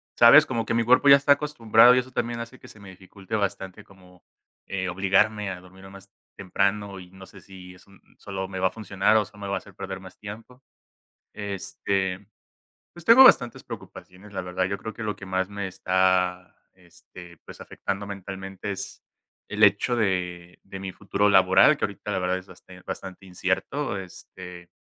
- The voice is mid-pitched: No, very low, 95 Hz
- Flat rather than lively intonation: Yes, narrow, 2.1 semitones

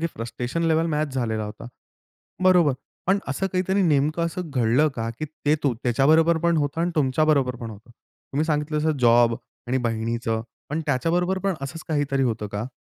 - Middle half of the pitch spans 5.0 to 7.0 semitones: Yes, average, 5.3 semitones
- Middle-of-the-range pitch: Yes, medium, 145 Hz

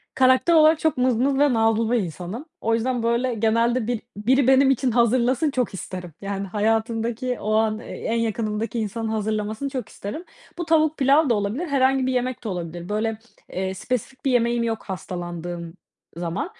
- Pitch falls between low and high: No, high, 230 Hz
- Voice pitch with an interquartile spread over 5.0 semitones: No, average, 3.6 semitones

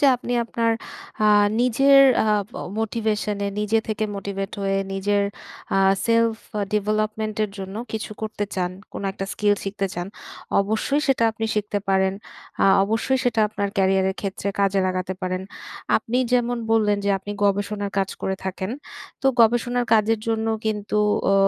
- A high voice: Yes, high, 210 Hz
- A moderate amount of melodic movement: No, narrow, 2.3 semitones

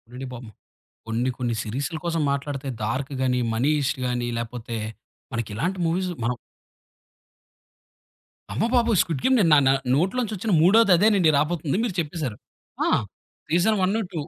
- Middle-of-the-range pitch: Yes, medium, 150 Hz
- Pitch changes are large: Yes, wide, 7.0 semitones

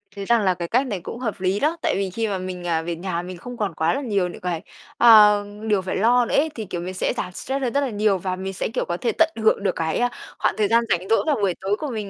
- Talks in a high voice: Yes, high, 200 Hz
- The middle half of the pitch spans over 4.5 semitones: No, average, 4.1 semitones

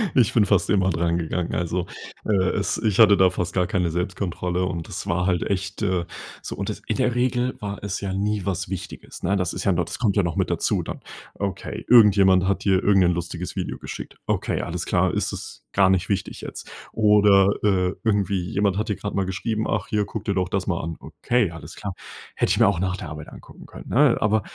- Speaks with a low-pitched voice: Yes, very low, 95 Hz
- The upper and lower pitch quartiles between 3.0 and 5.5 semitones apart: No, narrow, 2.4 semitones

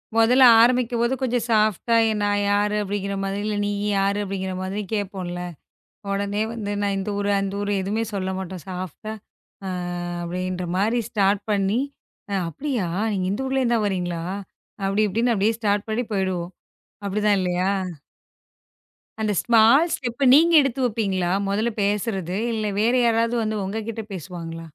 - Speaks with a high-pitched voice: Yes, high, 205 Hz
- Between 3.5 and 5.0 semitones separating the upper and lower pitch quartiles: No, average, 3.0 semitones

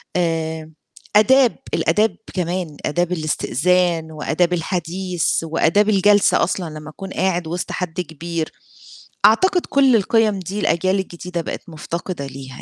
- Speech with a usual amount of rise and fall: Yes, average, 3.1 semitones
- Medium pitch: Yes, medium, 175 Hz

